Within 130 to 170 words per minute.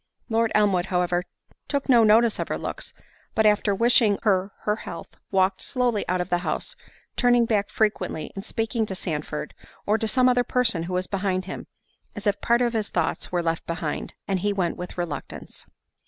No: average, 190 wpm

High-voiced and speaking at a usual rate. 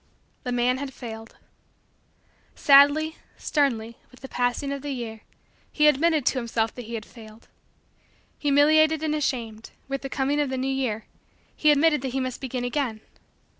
Yes: very high, 265 Hz; average, 165 wpm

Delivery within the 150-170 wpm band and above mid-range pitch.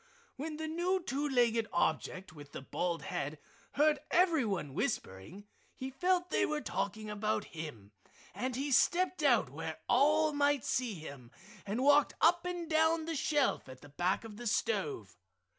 Yes: average, 160 wpm; high, 245 Hz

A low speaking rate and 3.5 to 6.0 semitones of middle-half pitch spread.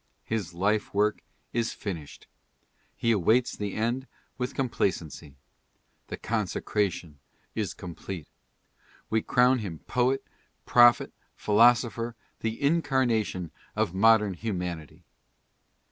Yes: slow, 100 wpm; average, 4.6 semitones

